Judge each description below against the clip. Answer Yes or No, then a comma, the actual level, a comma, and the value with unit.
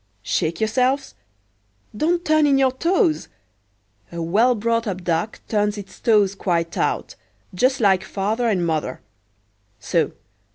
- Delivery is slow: Yes, slow, 120 wpm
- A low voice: No, high, 200 Hz